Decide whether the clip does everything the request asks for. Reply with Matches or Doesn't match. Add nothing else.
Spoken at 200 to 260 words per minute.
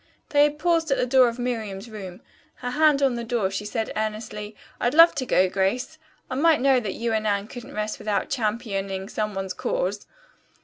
Matches